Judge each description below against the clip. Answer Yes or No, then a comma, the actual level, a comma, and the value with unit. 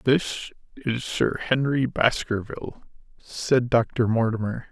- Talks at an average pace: No, slow, 100 wpm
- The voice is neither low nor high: No, low, 125 Hz